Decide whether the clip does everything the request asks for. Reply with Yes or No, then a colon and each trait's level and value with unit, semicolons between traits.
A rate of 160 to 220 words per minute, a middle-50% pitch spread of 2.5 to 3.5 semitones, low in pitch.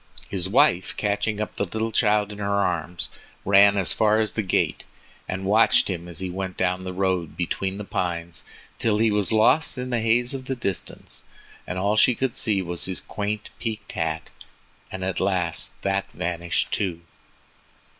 Yes: average, 175 wpm; average, 2.9 semitones; low, 100 Hz